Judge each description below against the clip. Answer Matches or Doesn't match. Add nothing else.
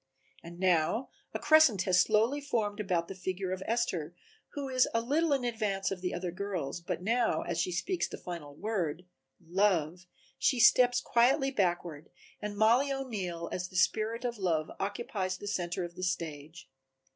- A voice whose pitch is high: Matches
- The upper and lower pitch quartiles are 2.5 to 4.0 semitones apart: Doesn't match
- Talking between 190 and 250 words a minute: Doesn't match